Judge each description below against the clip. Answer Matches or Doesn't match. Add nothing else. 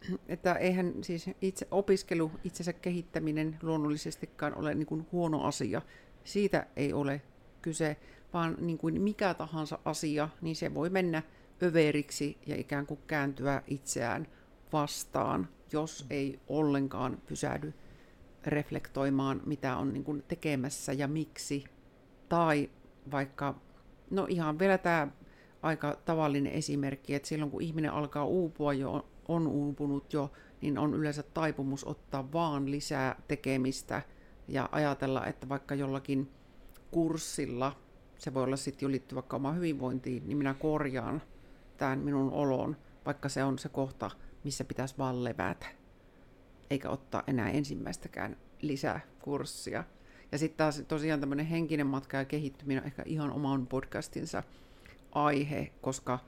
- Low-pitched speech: Doesn't match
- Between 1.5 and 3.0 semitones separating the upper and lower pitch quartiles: Matches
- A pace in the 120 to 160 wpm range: Matches